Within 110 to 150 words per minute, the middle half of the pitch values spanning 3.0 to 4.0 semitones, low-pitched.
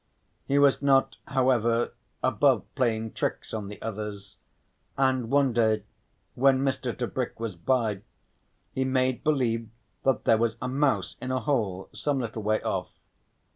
Yes: average, 145 wpm; average, 3.3 semitones; low, 120 Hz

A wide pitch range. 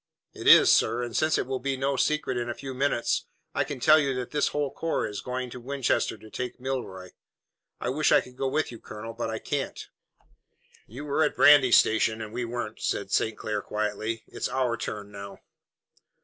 No: average, 3.6 semitones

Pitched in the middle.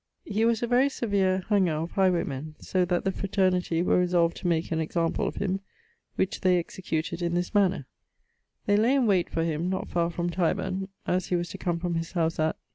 Yes: medium, 180 Hz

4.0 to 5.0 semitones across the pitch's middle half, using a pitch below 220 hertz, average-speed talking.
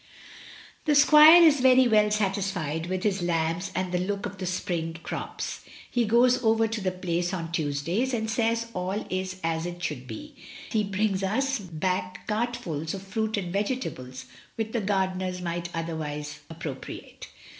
Yes: average, 4.4 semitones; high, 190 Hz; average, 165 wpm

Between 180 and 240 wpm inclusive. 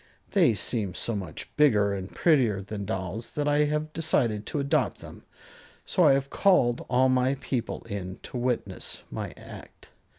No: average, 165 wpm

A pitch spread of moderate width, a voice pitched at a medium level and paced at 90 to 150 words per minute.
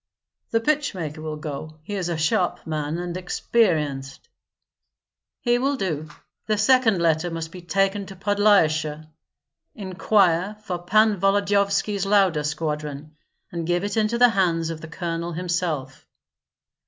Yes: average, 4.3 semitones; medium, 175 Hz; average, 140 wpm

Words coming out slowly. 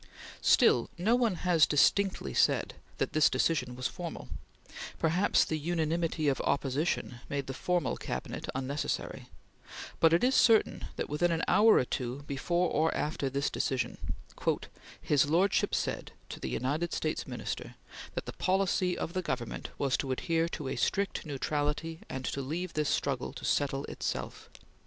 No: average, 155 wpm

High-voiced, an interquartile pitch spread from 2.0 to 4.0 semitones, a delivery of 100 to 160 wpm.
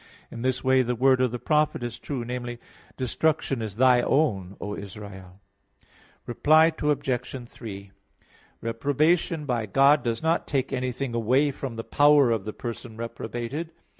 No: low, 125 Hz; average, 3.5 semitones; average, 150 wpm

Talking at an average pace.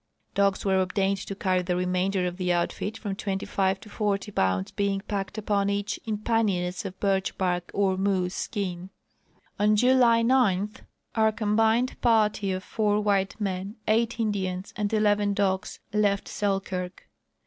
Yes: average, 160 wpm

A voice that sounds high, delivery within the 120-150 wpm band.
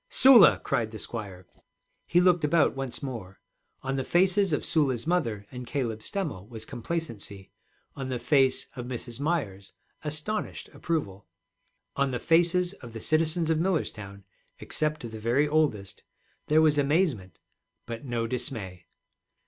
No: low, 135 Hz; average, 140 wpm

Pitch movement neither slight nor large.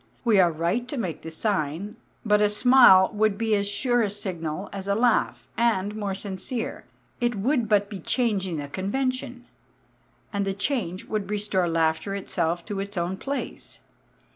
Yes: average, 3.3 semitones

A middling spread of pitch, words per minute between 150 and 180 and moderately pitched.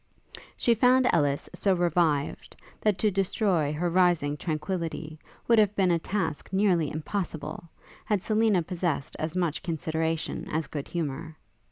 No: average, 3.9 semitones; average, 140 wpm; medium, 170 Hz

